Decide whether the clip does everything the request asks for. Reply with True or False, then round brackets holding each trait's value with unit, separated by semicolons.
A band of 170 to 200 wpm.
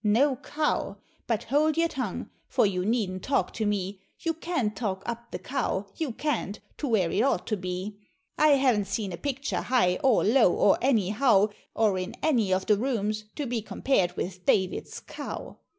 True (180 wpm)